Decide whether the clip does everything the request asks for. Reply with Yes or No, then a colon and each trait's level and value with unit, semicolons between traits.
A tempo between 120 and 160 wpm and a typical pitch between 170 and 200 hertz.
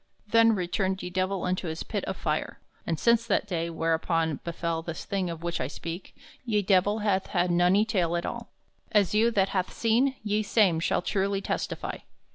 No: average, 190 wpm; medium, 185 Hz